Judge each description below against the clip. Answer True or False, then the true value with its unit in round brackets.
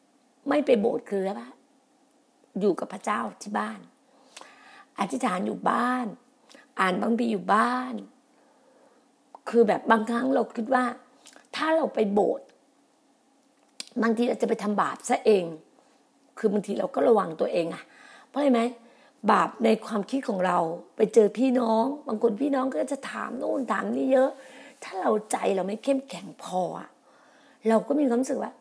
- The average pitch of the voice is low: False (250 Hz)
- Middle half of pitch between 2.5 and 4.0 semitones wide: True (3.4 semitones)